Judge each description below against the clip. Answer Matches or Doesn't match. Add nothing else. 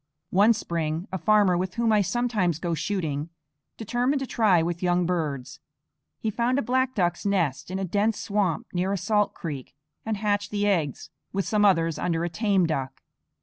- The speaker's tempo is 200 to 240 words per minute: Doesn't match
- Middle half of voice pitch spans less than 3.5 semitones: Doesn't match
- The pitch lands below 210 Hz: Matches